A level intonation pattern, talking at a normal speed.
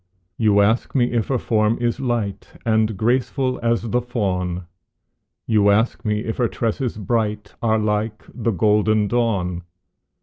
Yes: narrow, 2.2 semitones; average, 145 wpm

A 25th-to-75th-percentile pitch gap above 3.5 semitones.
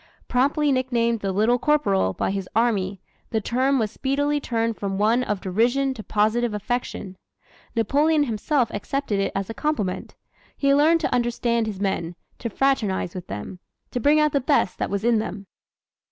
Yes: average, 5.3 semitones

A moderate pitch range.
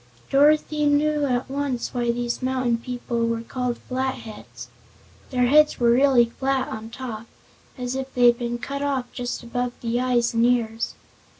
No: narrow, 2.0 semitones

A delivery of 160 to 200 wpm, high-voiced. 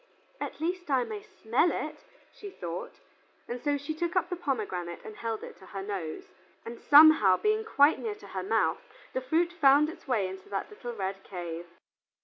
Yes: average, 185 wpm; very high, 260 Hz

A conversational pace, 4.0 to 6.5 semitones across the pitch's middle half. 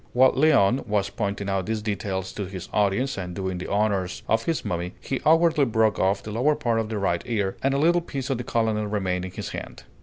No: fast, 235 wpm; average, 5.0 semitones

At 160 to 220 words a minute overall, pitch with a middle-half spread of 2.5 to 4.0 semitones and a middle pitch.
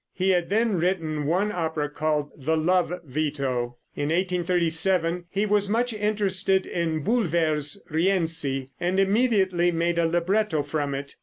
No: average, 140 wpm; average, 3.7 semitones; medium, 170 Hz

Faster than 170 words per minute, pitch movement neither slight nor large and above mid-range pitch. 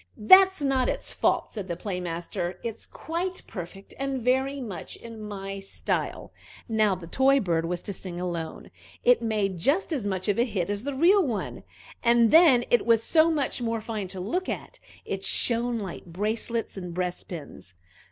No: average, 180 wpm; wide, 6.1 semitones; high, 220 Hz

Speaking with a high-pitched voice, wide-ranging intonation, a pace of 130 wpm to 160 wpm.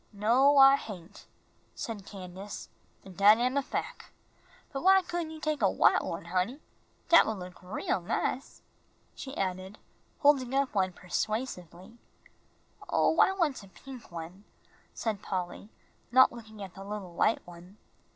Yes: high, 210 Hz; wide, 6.3 semitones; average, 150 wpm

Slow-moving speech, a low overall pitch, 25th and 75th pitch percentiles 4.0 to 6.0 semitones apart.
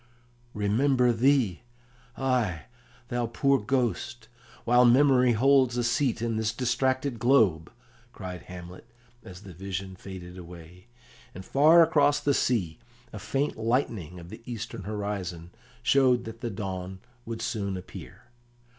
Yes: slow, 130 wpm; low, 115 Hz; wide, 5.4 semitones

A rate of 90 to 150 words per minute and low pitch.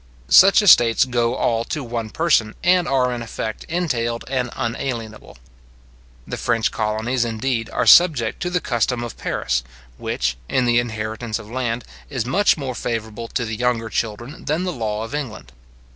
No: average, 165 wpm; low, 120 Hz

